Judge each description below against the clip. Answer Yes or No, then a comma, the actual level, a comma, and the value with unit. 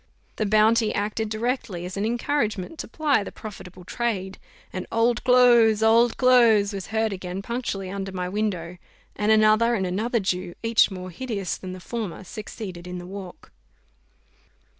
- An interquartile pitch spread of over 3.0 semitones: Yes, average, 3.7 semitones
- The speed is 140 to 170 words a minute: Yes, average, 160 wpm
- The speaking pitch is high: Yes, high, 210 Hz